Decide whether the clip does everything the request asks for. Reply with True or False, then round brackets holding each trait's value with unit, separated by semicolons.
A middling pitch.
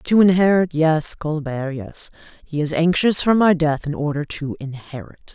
True (160 Hz)